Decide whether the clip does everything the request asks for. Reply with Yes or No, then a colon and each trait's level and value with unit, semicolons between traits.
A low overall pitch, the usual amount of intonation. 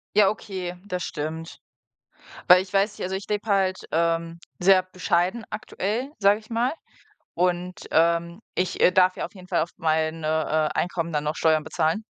No: medium, 180 Hz; average, 3.1 semitones